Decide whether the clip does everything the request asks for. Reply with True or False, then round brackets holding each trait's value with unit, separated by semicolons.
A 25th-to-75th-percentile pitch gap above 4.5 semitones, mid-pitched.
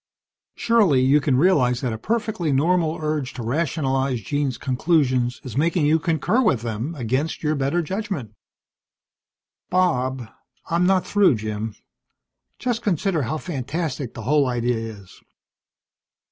True (5.3 semitones; 145 Hz)